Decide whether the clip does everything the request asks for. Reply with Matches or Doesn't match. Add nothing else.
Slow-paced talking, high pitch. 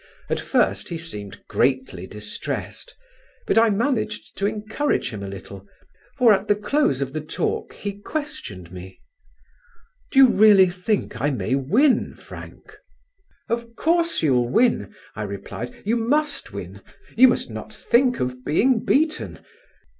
Doesn't match